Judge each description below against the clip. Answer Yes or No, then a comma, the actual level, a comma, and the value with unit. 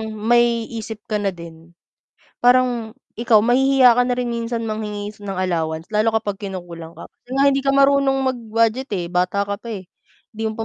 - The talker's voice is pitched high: Yes, high, 220 Hz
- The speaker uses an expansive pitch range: No, average, 3.7 semitones